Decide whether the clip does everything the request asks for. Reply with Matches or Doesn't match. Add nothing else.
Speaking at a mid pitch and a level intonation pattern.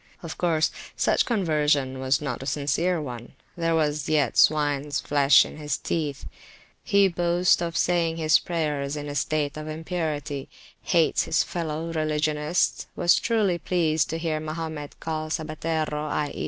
Matches